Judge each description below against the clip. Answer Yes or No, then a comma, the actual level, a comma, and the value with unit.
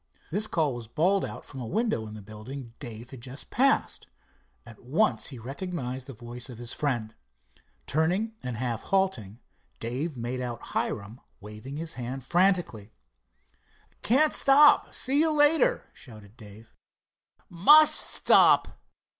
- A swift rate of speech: No, average, 140 wpm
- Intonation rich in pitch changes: Yes, wide, 8.3 semitones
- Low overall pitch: Yes, low, 130 Hz